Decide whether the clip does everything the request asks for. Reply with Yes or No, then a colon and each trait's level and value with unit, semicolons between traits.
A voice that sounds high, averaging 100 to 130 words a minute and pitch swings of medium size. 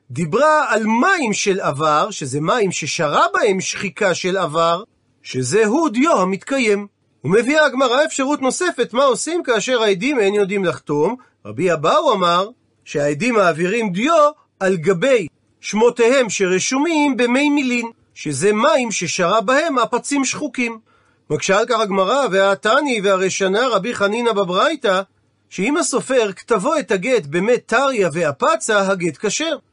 No: high, 215 Hz; average, 125 wpm; wide, 6.1 semitones